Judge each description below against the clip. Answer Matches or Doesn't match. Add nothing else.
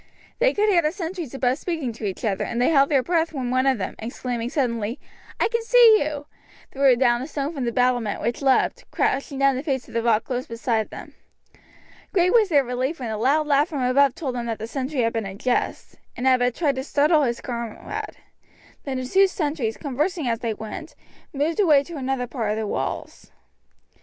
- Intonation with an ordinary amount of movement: Matches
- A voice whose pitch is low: Doesn't match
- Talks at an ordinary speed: Doesn't match